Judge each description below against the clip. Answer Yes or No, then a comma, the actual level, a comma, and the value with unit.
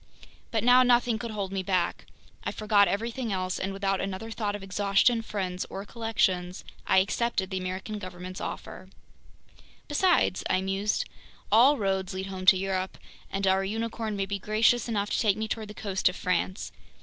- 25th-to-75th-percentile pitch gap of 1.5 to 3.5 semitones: Yes, average, 2.8 semitones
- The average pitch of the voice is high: Yes, high, 200 Hz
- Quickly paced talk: No, average, 175 wpm